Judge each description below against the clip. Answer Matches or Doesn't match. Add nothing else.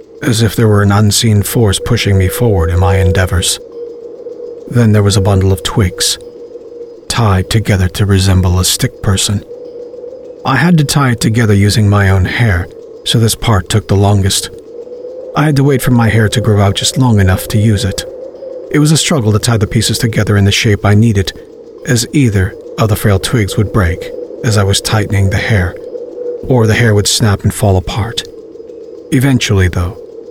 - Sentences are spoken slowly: Doesn't match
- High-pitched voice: Doesn't match